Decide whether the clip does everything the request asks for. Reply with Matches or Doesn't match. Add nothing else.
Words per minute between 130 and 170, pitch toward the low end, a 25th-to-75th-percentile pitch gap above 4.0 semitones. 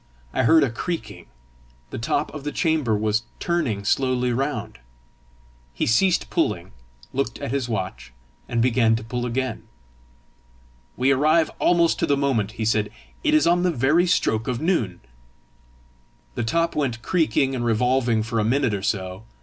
Matches